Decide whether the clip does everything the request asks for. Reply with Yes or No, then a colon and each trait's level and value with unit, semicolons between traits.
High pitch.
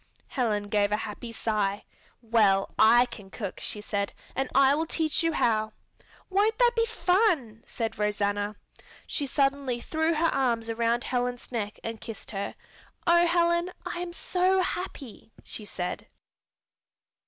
Yes: high, 240 Hz